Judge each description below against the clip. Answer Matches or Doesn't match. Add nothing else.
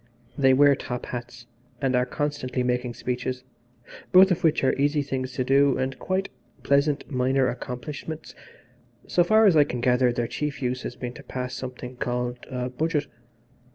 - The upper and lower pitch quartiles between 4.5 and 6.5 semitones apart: Doesn't match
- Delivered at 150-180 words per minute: Matches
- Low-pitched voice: Matches